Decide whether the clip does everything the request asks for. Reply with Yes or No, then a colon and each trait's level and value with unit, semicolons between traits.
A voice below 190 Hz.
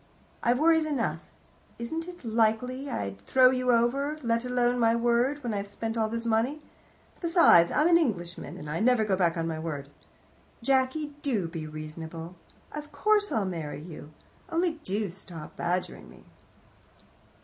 No: high, 230 Hz